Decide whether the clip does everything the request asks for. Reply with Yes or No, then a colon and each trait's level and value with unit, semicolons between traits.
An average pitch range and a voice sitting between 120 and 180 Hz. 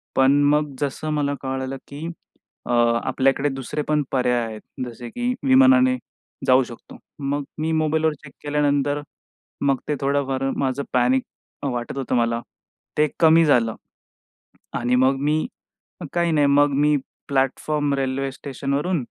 No: narrow, 2.3 semitones; medium, 140 Hz